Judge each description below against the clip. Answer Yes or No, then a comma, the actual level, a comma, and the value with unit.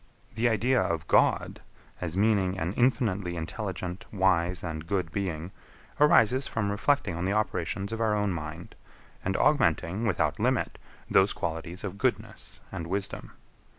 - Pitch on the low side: Yes, very low, 95 Hz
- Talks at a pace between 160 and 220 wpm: No, average, 145 wpm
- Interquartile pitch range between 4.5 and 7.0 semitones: No, average, 3.9 semitones